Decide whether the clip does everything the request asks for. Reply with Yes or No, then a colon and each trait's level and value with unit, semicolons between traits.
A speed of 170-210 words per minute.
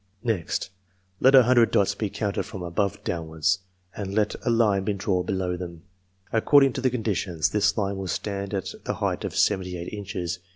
Yes: average, 195 wpm